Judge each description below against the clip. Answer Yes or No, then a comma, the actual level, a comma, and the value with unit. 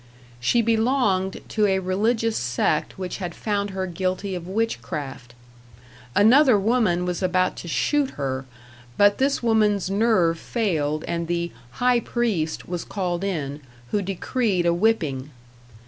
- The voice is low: No, high, 190 Hz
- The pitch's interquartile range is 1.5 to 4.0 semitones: No, average, 4.5 semitones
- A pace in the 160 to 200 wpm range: No, slow, 135 wpm